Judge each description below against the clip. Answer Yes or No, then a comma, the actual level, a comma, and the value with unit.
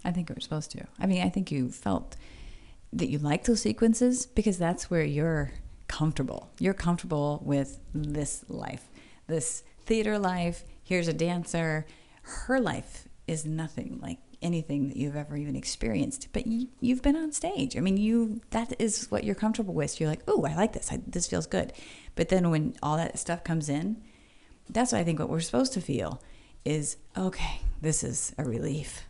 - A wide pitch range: Yes, wide, 6.2 semitones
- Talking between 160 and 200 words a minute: Yes, average, 190 wpm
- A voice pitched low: No, medium, 165 Hz